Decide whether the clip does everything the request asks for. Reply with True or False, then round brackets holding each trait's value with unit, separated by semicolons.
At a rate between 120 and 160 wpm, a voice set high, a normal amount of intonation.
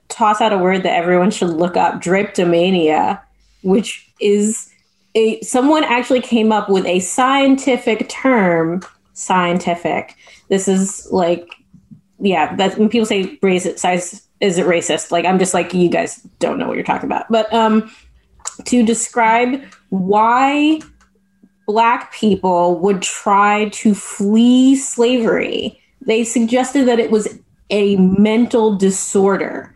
True (135 wpm; 205 Hz; 3.9 semitones)